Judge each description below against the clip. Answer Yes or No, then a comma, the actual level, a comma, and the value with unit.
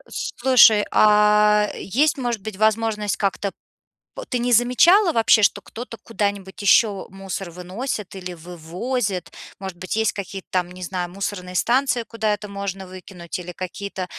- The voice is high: Yes, high, 200 Hz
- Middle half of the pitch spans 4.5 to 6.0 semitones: No, average, 3.5 semitones